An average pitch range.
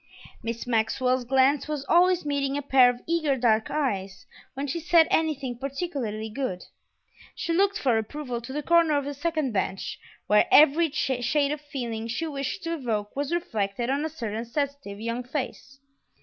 Yes: average, 4.4 semitones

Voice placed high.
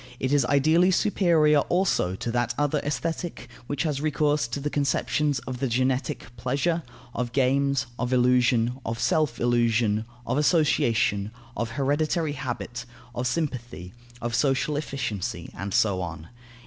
No: low, 130 Hz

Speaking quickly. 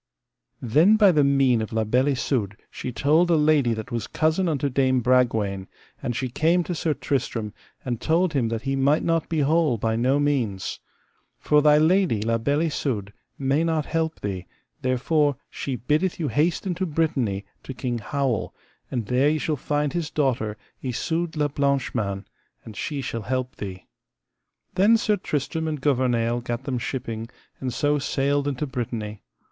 No: average, 175 wpm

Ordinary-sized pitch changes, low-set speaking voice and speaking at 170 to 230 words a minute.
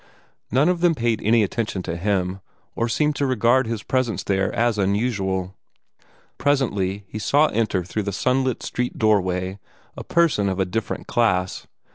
No: average, 4.7 semitones; low, 110 Hz; average, 160 wpm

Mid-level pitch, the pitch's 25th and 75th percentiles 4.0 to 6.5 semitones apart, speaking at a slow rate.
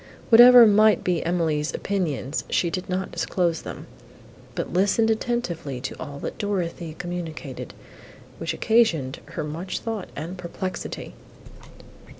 Yes: medium, 180 Hz; average, 4.3 semitones; slow, 125 wpm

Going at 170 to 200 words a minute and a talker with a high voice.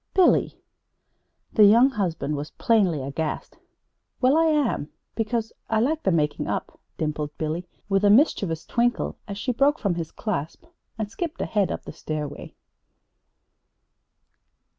No: average, 140 wpm; high, 205 Hz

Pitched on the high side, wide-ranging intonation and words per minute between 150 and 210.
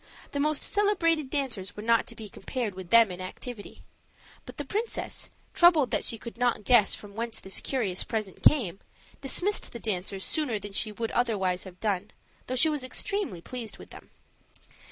Yes: high, 230 Hz; wide, 5.8 semitones; average, 180 wpm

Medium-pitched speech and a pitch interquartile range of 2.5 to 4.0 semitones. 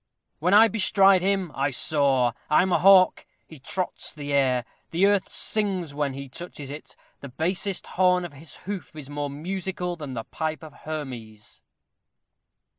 No: medium, 155 Hz; average, 5.0 semitones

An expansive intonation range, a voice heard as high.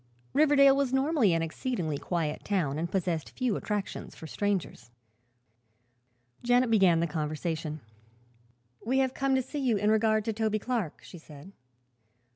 Yes: wide, 7.5 semitones; high, 205 Hz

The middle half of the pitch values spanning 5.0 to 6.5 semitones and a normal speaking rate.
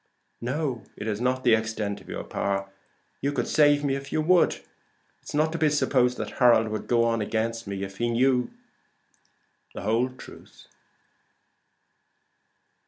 No: average, 3.9 semitones; average, 165 wpm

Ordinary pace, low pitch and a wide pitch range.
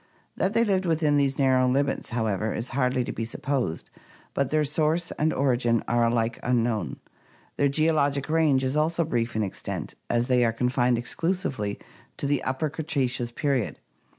No: average, 170 wpm; low, 130 Hz; average, 4.1 semitones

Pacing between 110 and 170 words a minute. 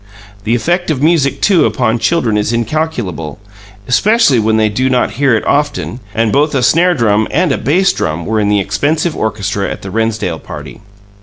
No: average, 185 wpm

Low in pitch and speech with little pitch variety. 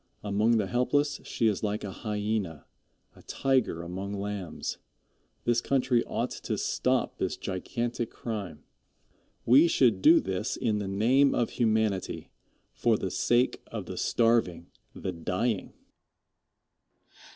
No: low, 110 Hz; average, 3.8 semitones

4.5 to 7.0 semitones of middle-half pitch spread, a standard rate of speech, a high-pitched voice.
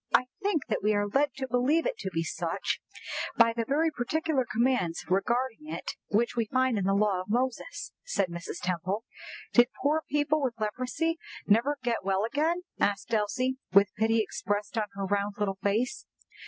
Yes: average, 4.8 semitones; average, 180 wpm; high, 230 Hz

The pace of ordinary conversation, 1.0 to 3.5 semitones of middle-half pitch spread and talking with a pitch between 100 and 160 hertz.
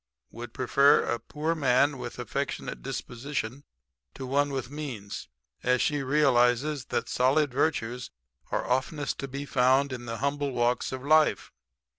Yes: average, 150 wpm; average, 2.7 semitones; low, 135 Hz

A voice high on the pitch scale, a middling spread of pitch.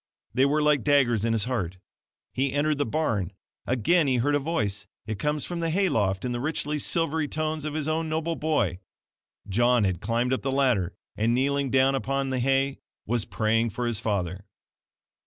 No: low, 130 Hz; average, 4.8 semitones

